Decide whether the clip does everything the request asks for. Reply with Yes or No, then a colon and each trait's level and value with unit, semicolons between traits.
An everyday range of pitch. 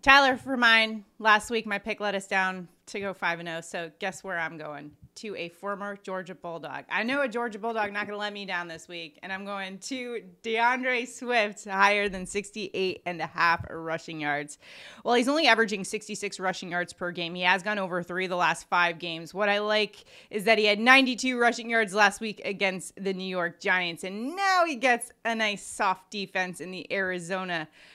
Yes: average, 3.8 semitones